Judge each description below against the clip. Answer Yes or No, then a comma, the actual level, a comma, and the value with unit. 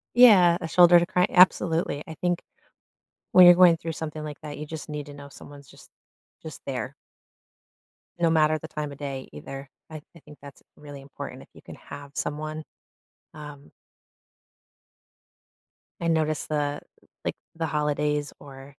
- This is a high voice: No, medium, 150 Hz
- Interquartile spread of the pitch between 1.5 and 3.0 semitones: Yes, narrow, 2.4 semitones